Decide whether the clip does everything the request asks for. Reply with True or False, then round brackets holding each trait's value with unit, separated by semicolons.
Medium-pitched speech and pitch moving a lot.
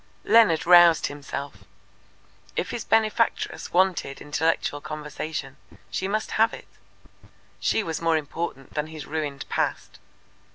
False (160 Hz; 4.2 semitones)